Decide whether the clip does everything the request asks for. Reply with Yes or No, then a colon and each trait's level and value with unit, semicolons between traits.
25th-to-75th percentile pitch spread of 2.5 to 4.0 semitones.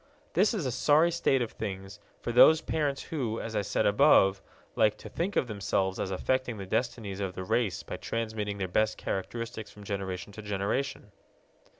No: average, 4.8 semitones